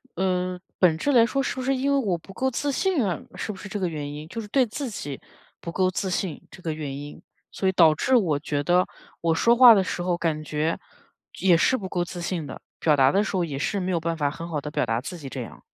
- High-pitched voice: No, medium, 180 Hz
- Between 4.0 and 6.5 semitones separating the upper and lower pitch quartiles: Yes, average, 5.1 semitones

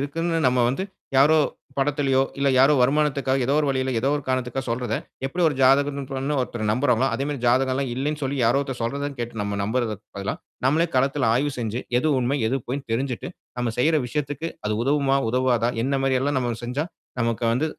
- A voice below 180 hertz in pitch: Yes, low, 135 Hz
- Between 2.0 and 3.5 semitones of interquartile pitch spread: Yes, narrow, 2.6 semitones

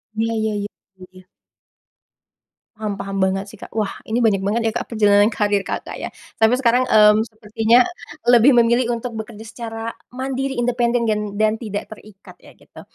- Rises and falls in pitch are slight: Yes, narrow, 2.1 semitones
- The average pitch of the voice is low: No, high, 220 Hz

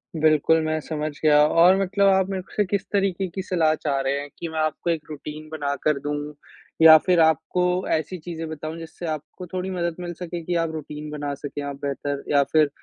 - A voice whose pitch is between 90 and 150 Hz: No, medium, 160 Hz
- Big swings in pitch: No, average, 3.0 semitones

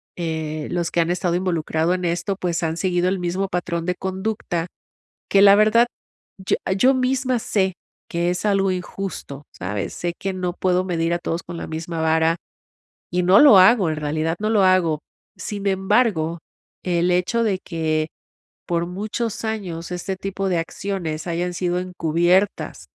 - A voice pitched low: No, medium, 180 Hz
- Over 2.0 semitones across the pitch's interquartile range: Yes, narrow, 2.6 semitones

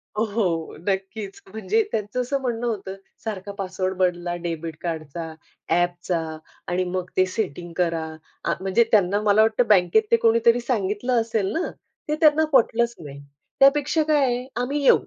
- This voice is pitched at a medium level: No, high, 205 Hz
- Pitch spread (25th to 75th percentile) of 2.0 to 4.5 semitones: No, average, 4.9 semitones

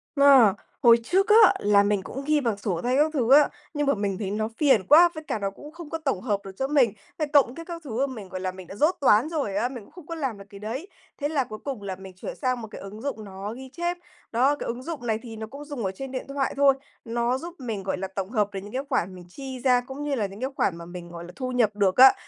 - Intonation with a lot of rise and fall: Yes, wide, 5.8 semitones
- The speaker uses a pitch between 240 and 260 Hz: Yes, high, 245 Hz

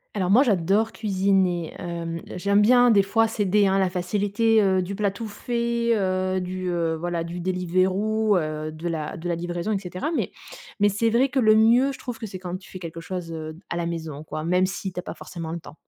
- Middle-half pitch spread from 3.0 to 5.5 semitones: Yes, average, 3.7 semitones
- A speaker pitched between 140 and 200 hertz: Yes, medium, 185 Hz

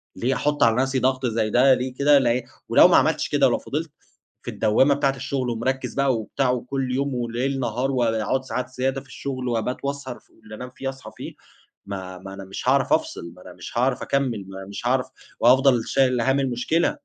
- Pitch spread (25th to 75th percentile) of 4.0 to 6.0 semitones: No, average, 2.7 semitones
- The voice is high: No, low, 125 Hz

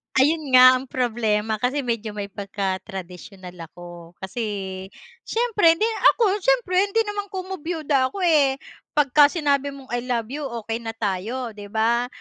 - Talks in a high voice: Yes, very high, 250 Hz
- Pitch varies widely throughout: Yes, wide, 6.5 semitones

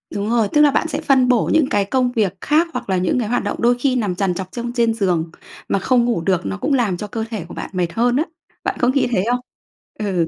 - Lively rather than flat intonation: No, average, 4.7 semitones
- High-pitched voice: Yes, high, 225 Hz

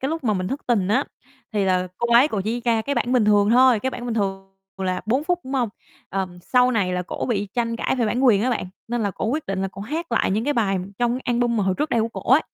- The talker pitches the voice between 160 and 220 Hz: No, high, 230 Hz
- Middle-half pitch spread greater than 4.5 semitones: No, average, 4.2 semitones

